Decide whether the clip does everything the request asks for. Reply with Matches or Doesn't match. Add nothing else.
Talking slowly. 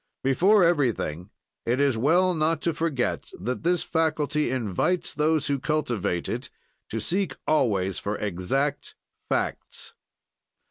Matches